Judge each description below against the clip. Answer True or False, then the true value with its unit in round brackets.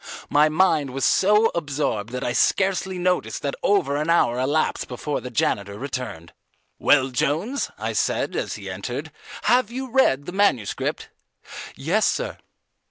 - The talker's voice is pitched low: False (150 Hz)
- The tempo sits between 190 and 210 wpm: False (150 wpm)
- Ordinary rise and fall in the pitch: False (6.8 semitones)